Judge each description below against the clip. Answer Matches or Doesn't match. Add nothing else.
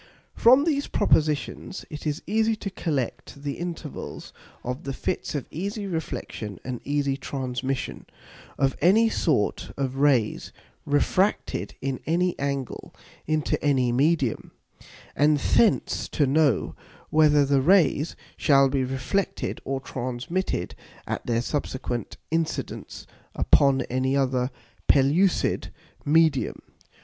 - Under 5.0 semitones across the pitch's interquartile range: Matches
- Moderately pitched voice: Matches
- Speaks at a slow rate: Matches